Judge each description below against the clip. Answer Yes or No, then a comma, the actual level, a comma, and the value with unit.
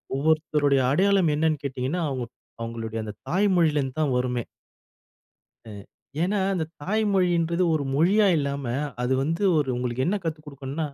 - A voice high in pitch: No, medium, 150 Hz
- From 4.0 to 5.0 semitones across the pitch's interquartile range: Yes, average, 4.4 semitones